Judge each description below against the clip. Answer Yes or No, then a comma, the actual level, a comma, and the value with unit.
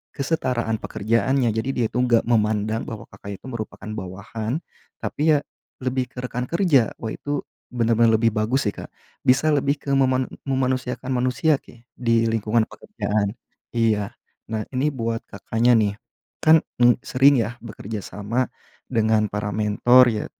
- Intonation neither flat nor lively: Yes, average, 3.0 semitones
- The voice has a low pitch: Yes, low, 115 Hz